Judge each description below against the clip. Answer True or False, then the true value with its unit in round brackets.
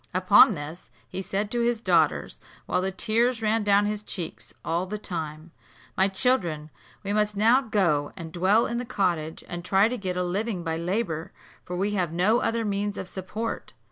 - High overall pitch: True (195 Hz)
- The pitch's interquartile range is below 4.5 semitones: True (3.7 semitones)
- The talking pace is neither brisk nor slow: True (190 wpm)